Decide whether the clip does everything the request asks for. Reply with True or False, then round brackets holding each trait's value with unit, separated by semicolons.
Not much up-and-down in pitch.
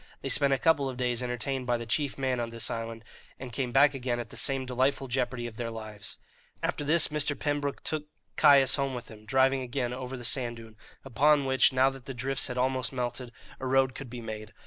True (2.2 semitones)